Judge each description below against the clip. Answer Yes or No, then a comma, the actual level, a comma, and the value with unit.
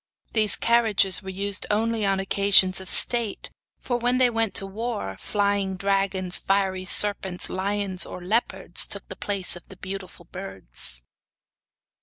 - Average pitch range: No, narrow, 2.1 semitones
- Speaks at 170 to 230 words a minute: No, average, 145 wpm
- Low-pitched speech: No, high, 195 Hz